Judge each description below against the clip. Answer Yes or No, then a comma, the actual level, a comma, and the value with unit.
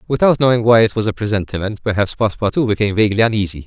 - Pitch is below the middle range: Yes, low, 110 Hz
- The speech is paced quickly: No, average, 195 wpm